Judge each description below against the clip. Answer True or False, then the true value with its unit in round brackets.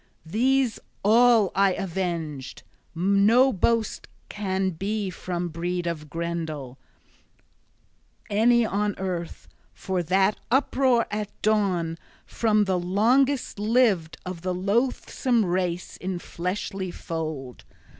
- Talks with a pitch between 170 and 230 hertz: True (190 Hz)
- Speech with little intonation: False (4.0 semitones)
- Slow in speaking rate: True (105 wpm)